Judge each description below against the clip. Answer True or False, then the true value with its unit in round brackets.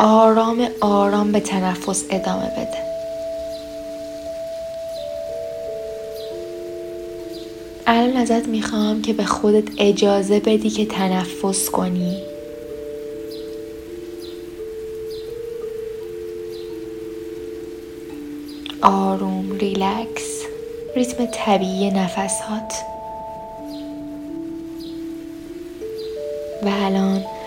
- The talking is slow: True (50 wpm)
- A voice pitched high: True (210 Hz)